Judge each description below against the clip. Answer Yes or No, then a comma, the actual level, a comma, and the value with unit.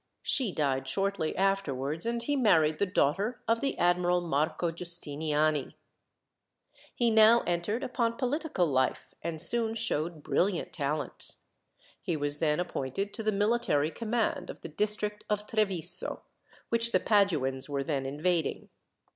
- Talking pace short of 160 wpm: Yes, average, 140 wpm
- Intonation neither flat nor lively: No, wide, 6.2 semitones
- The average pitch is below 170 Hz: No, medium, 180 Hz